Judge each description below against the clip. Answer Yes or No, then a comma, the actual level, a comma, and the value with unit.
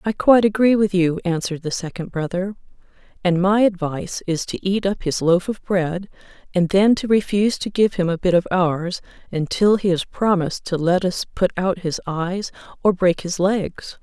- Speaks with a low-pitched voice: No, medium, 185 Hz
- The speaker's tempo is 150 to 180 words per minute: No, average, 195 wpm